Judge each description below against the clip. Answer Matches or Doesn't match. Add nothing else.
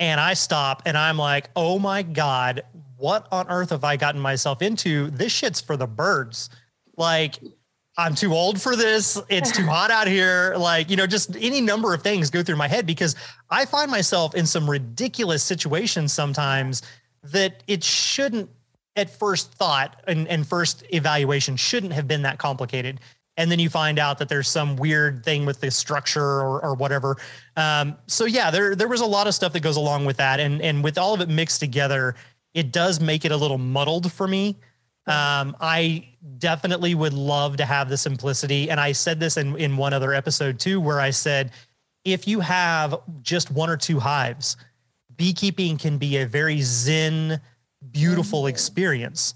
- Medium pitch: Matches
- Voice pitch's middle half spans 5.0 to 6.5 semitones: Doesn't match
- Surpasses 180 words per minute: Matches